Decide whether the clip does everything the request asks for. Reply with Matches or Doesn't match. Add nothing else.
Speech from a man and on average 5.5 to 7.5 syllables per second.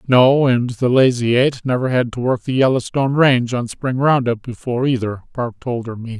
Matches